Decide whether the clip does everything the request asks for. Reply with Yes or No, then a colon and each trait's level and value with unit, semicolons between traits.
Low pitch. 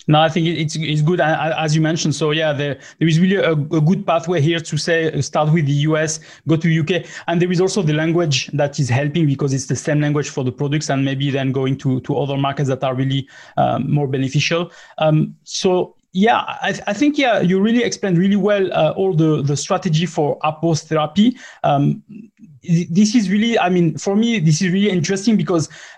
No: medium, 160 Hz